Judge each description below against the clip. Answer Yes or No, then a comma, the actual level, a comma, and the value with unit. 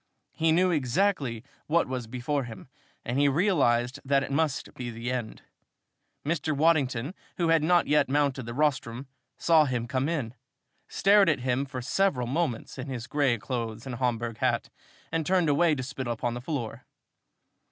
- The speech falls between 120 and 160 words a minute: No, average, 170 wpm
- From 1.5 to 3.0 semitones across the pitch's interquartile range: No, average, 4.3 semitones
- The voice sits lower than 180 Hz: Yes, low, 135 Hz